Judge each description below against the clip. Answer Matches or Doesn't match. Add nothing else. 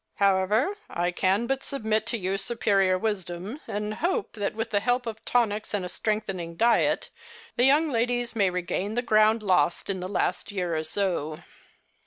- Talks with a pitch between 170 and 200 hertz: Doesn't match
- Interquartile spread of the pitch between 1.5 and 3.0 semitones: Doesn't match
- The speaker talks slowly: Doesn't match